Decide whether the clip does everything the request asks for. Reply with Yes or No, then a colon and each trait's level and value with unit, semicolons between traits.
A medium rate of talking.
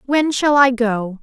Yes: average, 195 wpm